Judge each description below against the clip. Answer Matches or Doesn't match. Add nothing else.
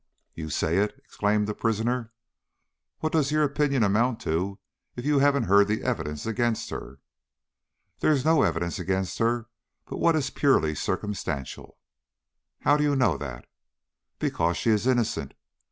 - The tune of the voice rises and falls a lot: Matches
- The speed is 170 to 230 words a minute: Doesn't match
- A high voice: Doesn't match